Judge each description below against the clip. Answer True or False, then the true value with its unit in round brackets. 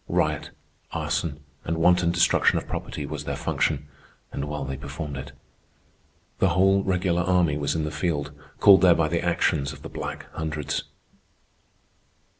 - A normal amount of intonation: True (3.4 semitones)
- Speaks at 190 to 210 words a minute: False (155 wpm)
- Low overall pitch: True (80 Hz)